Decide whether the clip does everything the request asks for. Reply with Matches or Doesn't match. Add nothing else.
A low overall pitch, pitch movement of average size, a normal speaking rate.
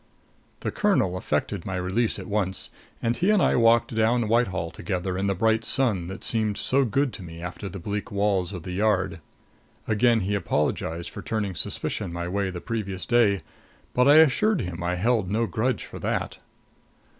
Matches